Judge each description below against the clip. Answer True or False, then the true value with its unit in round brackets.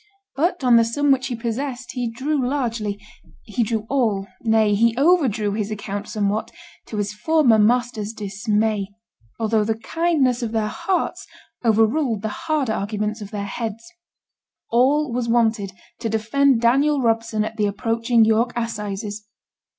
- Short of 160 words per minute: True (150 wpm)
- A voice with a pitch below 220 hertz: False (225 Hz)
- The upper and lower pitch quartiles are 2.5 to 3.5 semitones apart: True (2.8 semitones)